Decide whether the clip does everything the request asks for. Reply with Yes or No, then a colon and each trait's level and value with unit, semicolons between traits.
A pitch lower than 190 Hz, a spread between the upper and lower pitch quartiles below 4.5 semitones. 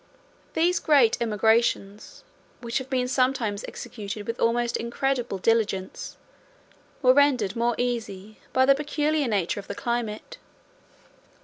No: high, 235 Hz; average, 3.5 semitones